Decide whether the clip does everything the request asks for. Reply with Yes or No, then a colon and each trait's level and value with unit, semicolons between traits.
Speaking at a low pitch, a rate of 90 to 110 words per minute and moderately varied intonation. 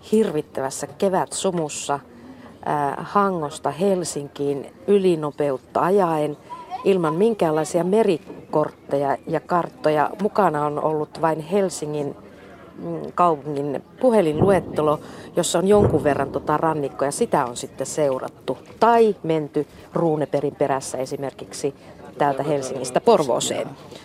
No: medium, 155 Hz; slow, 95 wpm; average, 4.2 semitones